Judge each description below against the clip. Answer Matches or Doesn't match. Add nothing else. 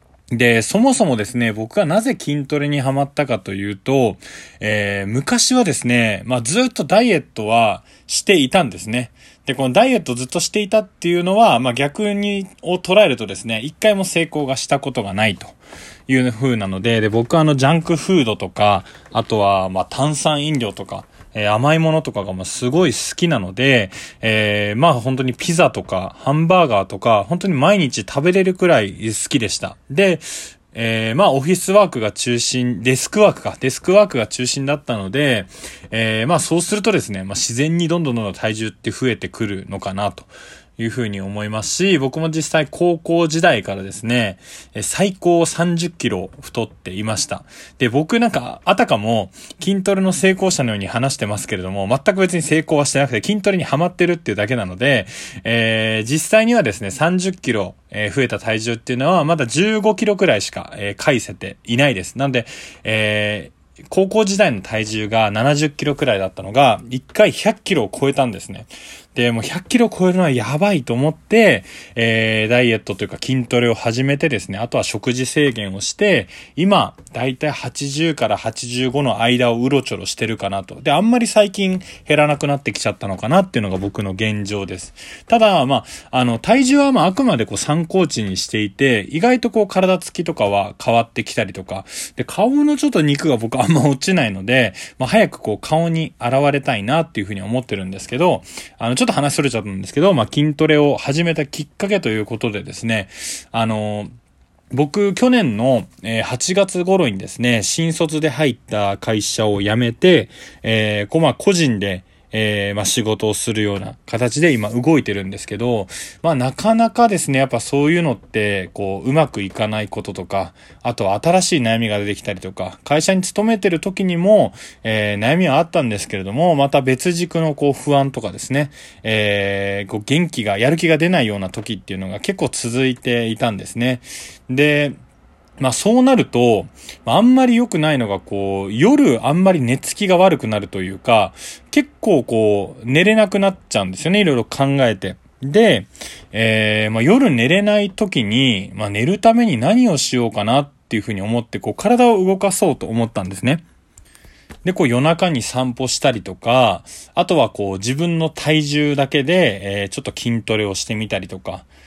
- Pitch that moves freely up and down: Matches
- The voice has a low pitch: Matches